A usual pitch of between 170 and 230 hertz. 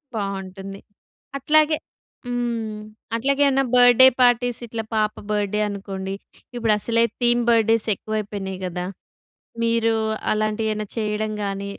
Yes: high, 215 Hz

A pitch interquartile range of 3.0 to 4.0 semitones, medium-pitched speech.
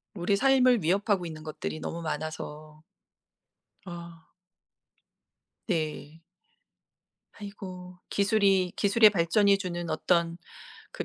Yes: average, 3.6 semitones; medium, 180 Hz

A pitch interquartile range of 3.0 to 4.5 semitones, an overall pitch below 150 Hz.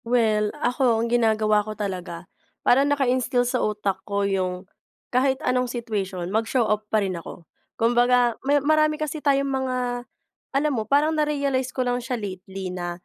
No: average, 3.9 semitones; high, 240 Hz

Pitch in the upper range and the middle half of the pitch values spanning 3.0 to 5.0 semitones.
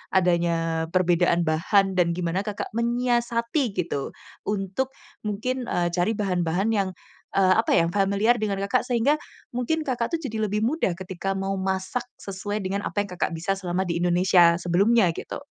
Yes: high, 195 Hz; average, 4.4 semitones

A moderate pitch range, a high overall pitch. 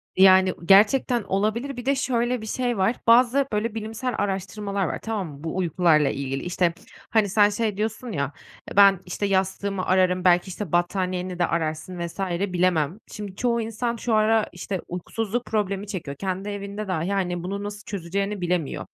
Yes: average, 3.3 semitones; high, 195 Hz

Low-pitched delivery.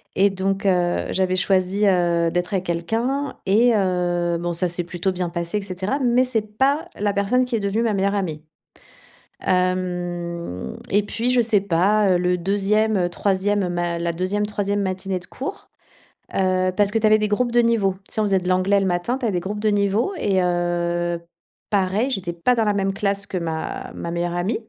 No: high, 195 Hz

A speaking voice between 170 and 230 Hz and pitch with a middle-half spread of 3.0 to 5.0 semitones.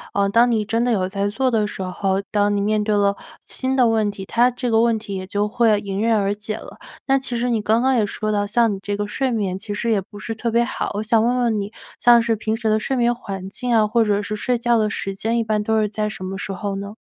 No: high, 215 Hz; narrow, 2.4 semitones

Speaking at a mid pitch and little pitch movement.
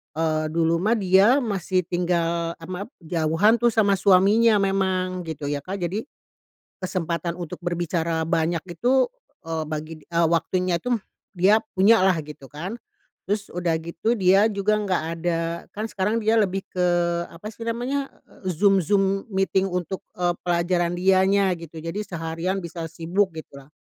No: medium, 180 Hz; average, 3.2 semitones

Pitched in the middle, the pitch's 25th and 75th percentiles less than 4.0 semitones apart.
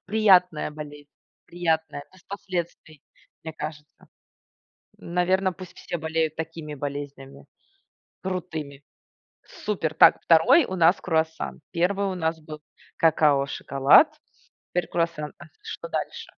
Yes: medium, 160 Hz; average, 3.3 semitones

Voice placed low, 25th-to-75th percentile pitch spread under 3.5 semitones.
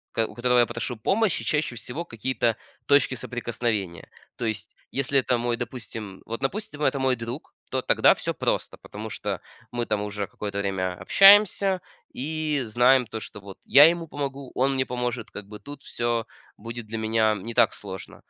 No: low, 120 Hz; average, 3.8 semitones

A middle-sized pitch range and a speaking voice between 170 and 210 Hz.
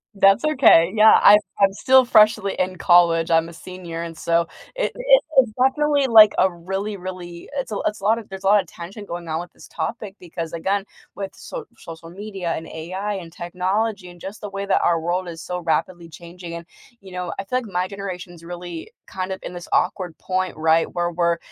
Yes: average, 3.0 semitones; medium, 185 Hz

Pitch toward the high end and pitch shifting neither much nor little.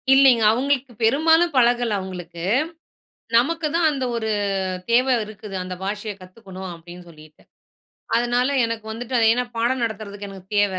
Yes: high, 225 Hz; average, 4.4 semitones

